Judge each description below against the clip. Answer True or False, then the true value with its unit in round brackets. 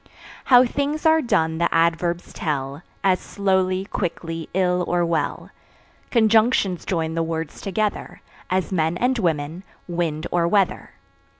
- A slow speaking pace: True (130 wpm)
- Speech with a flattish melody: False (3.6 semitones)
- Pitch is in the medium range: True (175 Hz)